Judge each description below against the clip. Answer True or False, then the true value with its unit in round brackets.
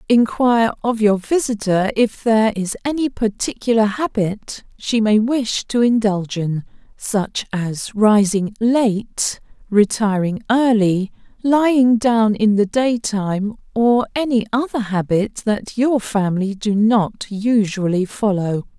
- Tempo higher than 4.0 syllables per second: False (3.9 syllables/s)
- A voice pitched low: False (215 Hz)